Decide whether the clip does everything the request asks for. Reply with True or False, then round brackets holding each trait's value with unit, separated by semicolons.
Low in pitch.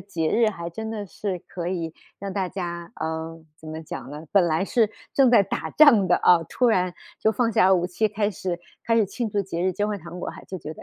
False (185 Hz)